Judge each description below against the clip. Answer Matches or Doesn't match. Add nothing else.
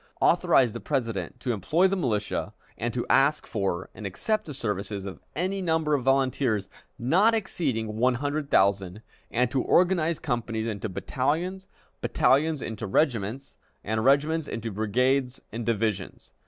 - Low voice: Matches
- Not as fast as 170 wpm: Matches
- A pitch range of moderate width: Doesn't match